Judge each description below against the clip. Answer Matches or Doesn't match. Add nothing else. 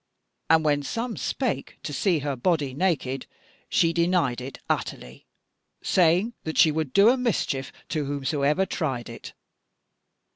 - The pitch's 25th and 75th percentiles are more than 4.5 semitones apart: Matches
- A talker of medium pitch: Matches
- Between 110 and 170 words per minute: Matches